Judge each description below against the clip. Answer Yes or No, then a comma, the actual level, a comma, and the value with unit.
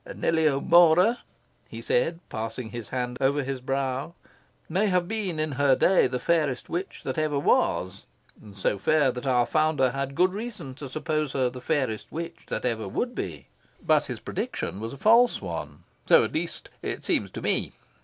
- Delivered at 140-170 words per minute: No, average, 180 wpm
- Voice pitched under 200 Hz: Yes, medium, 140 Hz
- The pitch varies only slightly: No, average, 5.2 semitones